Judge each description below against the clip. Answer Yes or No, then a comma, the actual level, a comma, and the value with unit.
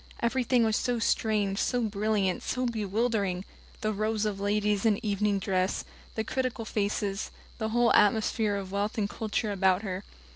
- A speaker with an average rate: Yes, average, 155 wpm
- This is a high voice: Yes, high, 210 Hz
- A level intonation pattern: Yes, narrow, 1.9 semitones